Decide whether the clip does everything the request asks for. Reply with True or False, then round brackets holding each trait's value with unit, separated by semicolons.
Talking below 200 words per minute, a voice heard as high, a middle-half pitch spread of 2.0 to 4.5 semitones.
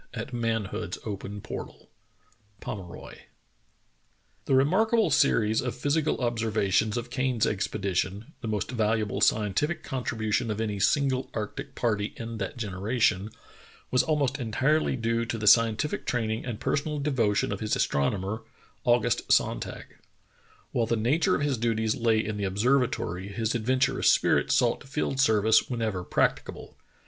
False (140 wpm; 115 Hz; 3.3 semitones)